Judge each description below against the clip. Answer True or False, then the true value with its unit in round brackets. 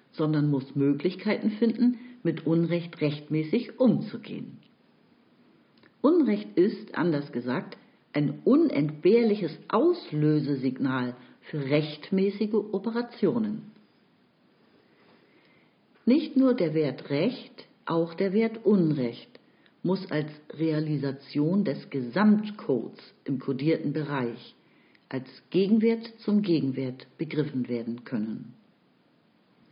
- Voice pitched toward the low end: False (165 Hz)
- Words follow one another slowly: True (85 wpm)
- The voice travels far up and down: True (6.9 semitones)